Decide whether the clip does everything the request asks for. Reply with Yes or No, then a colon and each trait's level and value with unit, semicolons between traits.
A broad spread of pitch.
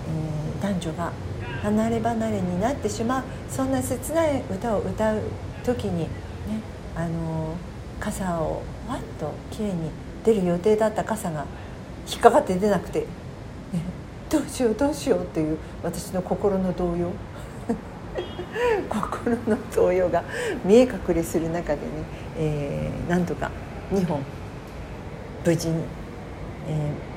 Yes: wide, 6.1 semitones